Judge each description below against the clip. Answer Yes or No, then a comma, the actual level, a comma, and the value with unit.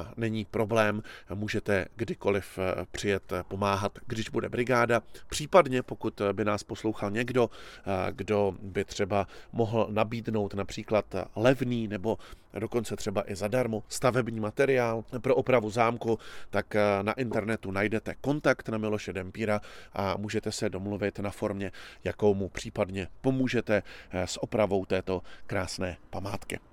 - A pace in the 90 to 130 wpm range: Yes, average, 125 wpm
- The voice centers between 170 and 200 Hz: No, low, 105 Hz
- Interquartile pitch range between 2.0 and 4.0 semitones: Yes, narrow, 2.5 semitones